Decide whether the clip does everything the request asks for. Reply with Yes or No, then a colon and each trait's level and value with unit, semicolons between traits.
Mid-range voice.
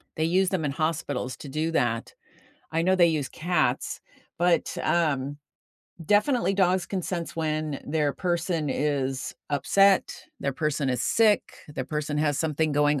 Yes: medium, 155 Hz